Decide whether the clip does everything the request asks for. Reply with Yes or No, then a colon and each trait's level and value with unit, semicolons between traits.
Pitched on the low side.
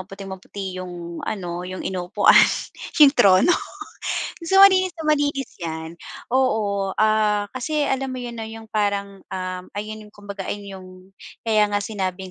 No: high, 205 Hz